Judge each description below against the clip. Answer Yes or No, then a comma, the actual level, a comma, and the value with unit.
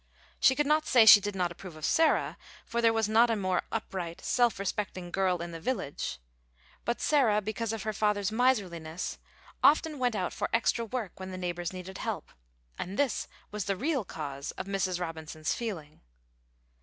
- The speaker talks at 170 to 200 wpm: Yes, average, 180 wpm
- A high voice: Yes, high, 200 Hz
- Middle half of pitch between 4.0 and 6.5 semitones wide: Yes, average, 4.6 semitones